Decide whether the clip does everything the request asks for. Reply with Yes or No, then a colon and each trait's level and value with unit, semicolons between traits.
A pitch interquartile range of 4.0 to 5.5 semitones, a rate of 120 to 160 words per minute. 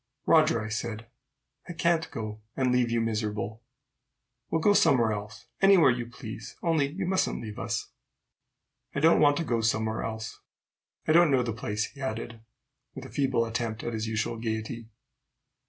No: average, 4.6 semitones; average, 170 wpm